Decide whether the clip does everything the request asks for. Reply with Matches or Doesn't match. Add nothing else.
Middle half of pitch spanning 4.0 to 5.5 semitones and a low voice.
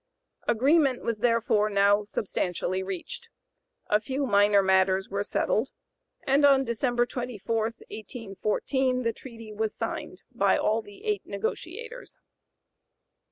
Doesn't match